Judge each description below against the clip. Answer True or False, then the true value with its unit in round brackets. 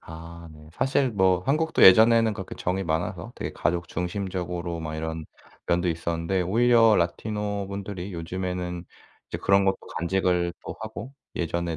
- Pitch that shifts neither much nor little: True (3.1 semitones)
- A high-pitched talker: False (90 Hz)